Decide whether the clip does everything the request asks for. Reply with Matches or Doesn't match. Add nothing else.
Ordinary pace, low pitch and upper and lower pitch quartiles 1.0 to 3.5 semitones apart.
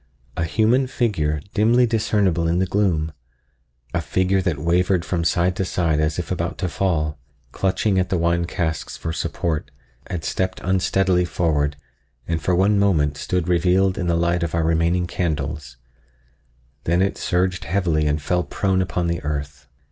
Matches